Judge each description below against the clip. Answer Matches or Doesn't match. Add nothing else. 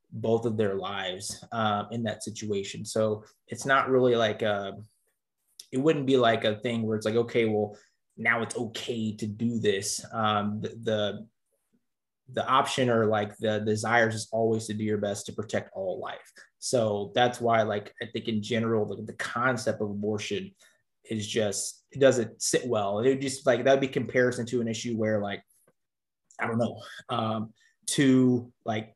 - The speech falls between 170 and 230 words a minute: Matches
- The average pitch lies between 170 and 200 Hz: Doesn't match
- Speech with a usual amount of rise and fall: Doesn't match